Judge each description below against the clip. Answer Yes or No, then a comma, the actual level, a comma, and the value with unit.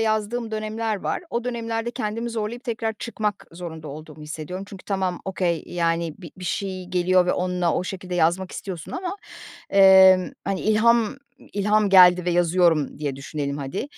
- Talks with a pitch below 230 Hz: Yes, high, 190 Hz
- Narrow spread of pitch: No, average, 3.9 semitones